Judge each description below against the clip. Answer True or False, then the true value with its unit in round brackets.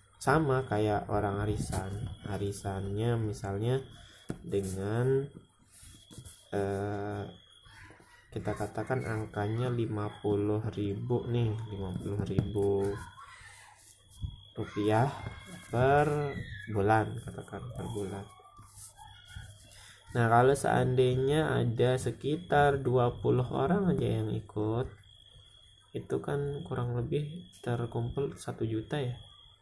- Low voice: True (110 Hz)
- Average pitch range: True (3.2 semitones)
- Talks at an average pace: False (80 wpm)